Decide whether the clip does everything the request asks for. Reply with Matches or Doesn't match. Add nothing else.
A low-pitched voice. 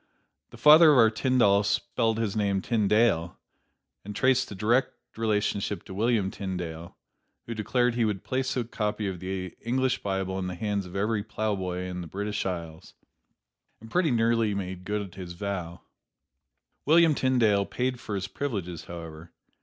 Matches